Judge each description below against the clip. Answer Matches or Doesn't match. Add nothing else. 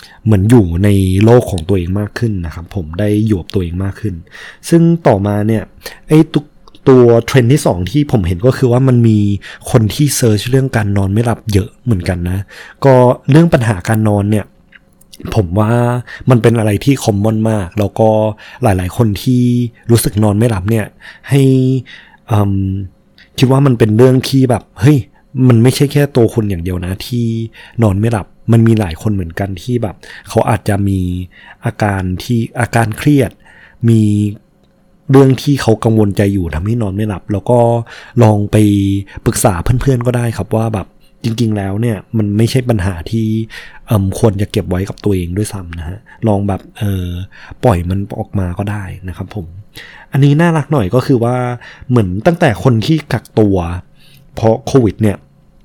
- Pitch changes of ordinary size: Matches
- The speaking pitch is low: Matches